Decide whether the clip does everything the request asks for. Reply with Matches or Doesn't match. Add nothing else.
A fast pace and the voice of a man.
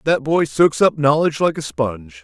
Matches